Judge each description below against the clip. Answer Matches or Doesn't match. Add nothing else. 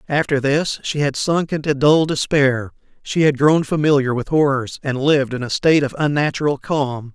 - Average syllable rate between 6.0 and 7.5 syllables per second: Doesn't match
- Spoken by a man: Matches